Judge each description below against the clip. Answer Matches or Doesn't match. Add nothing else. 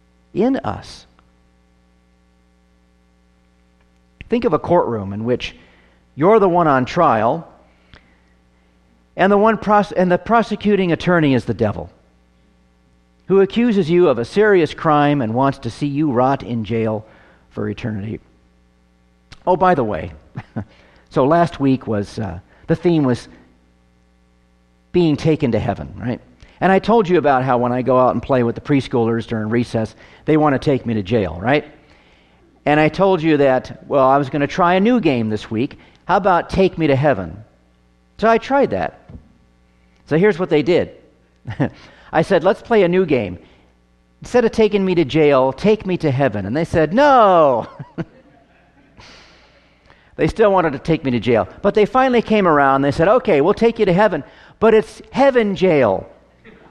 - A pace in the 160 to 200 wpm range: Matches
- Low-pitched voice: Matches